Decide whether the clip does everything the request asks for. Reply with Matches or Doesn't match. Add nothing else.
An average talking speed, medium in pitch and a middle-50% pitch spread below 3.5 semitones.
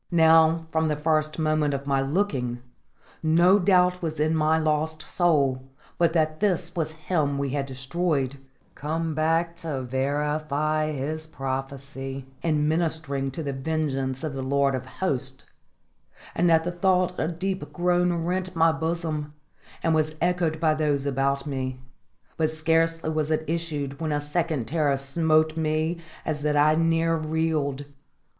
Matches